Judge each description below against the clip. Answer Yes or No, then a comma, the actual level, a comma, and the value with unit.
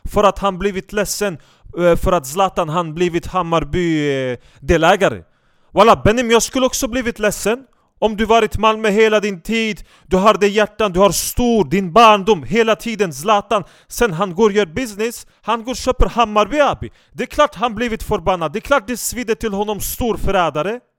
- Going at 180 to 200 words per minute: Yes, average, 190 wpm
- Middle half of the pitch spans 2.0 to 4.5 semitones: Yes, average, 3.3 semitones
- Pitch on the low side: No, high, 210 Hz